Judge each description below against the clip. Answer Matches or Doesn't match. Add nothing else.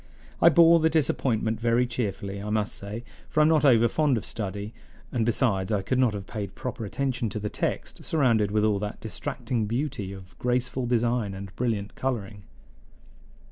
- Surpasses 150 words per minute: Matches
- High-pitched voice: Doesn't match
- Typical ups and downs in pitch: Matches